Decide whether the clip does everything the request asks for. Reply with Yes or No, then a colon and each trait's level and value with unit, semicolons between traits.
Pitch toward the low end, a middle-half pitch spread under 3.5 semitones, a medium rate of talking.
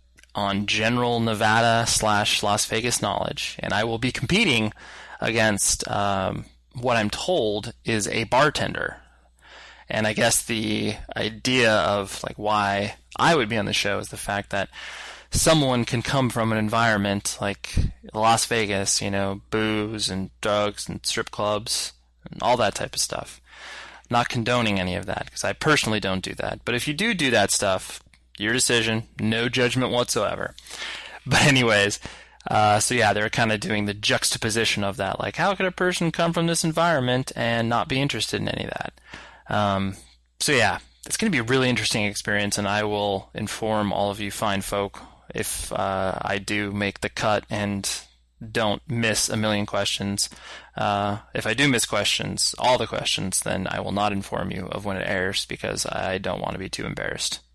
Yes: low, 105 Hz; average, 2.8 semitones; average, 180 wpm